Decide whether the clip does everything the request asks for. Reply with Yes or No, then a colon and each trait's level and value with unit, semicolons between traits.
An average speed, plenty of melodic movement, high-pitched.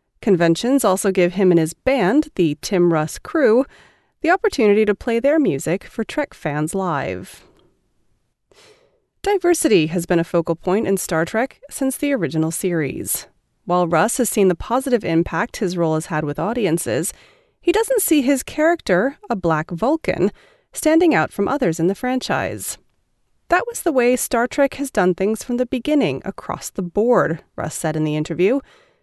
Yes: average, 170 wpm; wide, 8.7 semitones; high, 215 Hz